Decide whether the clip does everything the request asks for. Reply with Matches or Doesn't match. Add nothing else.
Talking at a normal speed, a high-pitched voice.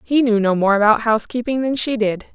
Doesn't match